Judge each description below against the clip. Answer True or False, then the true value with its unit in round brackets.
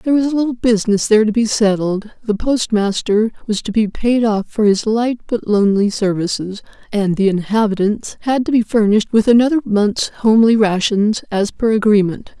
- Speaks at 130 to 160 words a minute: False (175 wpm)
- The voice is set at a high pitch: True (215 Hz)